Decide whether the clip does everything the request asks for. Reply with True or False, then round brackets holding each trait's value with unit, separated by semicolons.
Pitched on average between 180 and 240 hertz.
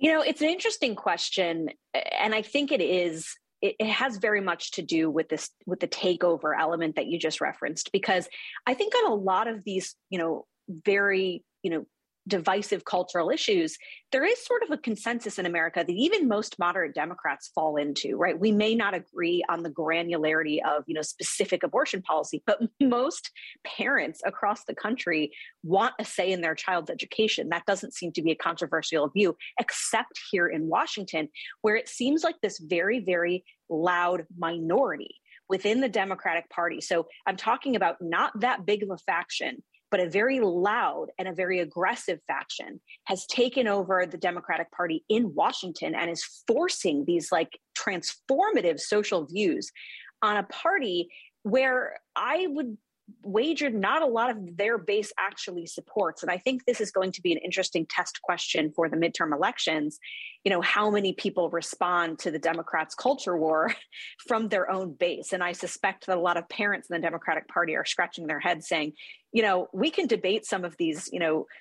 True (185 Hz)